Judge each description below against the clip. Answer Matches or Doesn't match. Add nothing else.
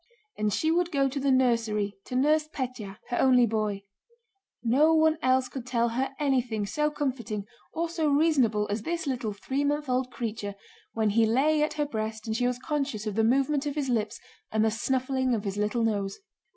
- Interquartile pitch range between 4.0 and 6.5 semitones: Matches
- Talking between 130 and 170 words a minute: Doesn't match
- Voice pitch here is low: Doesn't match